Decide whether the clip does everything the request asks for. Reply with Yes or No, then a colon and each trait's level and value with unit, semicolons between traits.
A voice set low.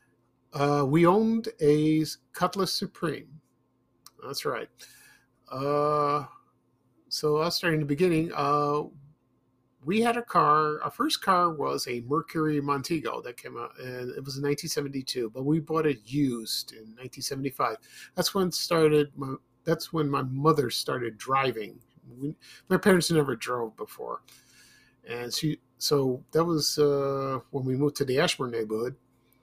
No: medium, 145 Hz